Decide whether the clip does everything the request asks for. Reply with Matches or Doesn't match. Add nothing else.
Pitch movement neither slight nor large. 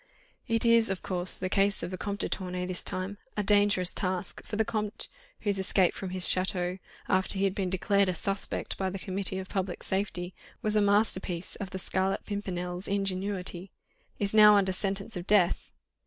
Doesn't match